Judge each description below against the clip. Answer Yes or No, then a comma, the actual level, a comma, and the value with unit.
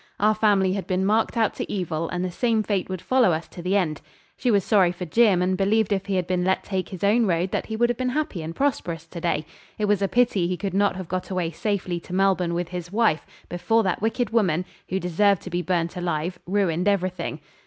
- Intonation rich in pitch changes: No, average, 2.9 semitones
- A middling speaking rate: No, fast, 245 wpm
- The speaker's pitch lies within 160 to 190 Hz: Yes, medium, 185 Hz